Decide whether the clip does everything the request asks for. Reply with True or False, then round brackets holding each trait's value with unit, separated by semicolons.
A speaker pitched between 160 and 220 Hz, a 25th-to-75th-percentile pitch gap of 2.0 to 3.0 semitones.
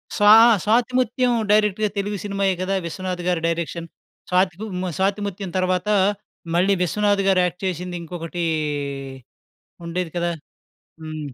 True (185 Hz; 2.7 semitones)